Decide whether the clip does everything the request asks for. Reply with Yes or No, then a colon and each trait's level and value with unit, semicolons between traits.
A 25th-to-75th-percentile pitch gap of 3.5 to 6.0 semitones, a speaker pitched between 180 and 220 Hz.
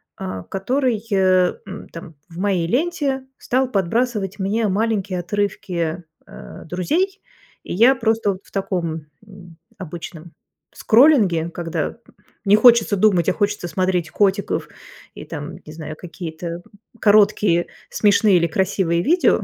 Yes: average, 4.1 semitones; high, 190 Hz